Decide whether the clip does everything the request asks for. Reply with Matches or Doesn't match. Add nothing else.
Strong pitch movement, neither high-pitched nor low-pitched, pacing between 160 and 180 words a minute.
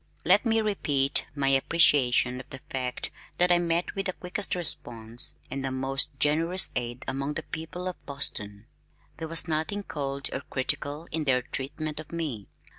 Doesn't match